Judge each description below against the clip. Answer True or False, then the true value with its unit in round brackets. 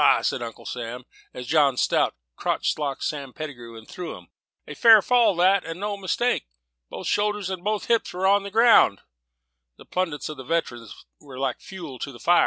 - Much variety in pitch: True (7.5 semitones)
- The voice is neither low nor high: True (165 Hz)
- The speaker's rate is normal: True (190 wpm)